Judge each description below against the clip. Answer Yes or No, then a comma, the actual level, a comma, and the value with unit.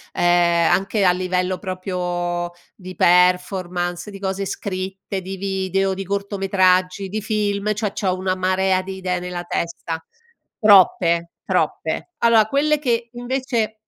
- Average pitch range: No, narrow, 1.8 semitones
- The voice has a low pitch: No, high, 190 Hz